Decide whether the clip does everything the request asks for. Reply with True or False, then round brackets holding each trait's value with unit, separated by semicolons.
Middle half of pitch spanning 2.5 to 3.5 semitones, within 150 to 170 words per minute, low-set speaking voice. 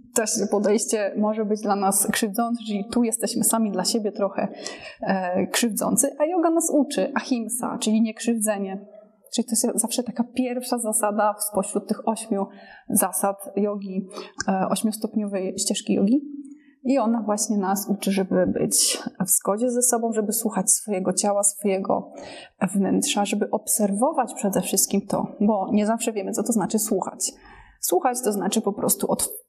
False (2.9 semitones; 155 wpm; 215 Hz)